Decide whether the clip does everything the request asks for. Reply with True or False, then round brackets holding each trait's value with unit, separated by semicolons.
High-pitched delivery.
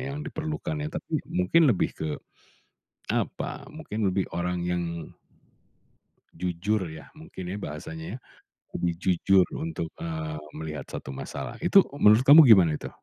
False (95 Hz)